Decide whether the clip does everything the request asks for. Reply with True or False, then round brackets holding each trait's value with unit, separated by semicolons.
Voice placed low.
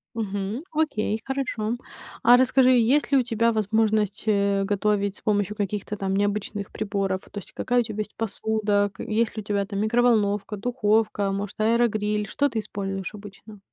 False (210 Hz)